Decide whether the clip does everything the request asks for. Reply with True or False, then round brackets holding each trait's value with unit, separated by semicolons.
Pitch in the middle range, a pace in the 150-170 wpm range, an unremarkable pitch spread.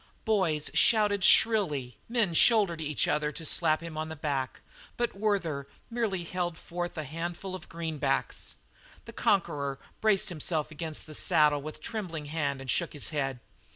True (165 Hz; 160 wpm; 4.4 semitones)